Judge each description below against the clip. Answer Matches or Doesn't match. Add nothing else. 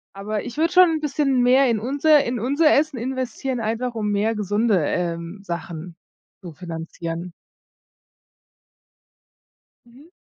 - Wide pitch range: Matches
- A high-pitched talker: Matches